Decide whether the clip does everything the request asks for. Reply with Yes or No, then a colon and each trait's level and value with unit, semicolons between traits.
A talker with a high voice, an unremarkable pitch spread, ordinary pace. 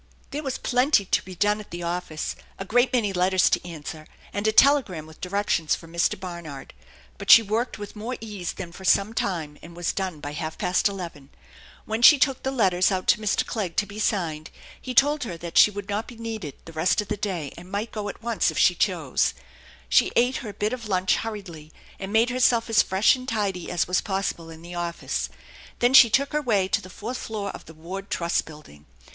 No: high, 195 Hz; average, 4.6 semitones; fast, 235 wpm